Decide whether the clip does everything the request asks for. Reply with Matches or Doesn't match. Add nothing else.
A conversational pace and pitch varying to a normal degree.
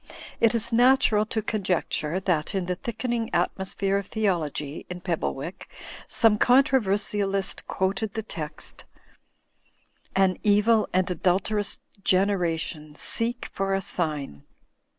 Doesn't match